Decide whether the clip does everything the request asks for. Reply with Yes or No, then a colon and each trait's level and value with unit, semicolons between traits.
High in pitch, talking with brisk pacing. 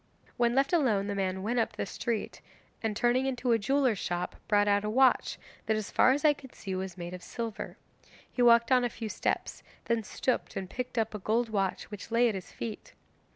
Yes: high, 225 Hz; fast, 220 wpm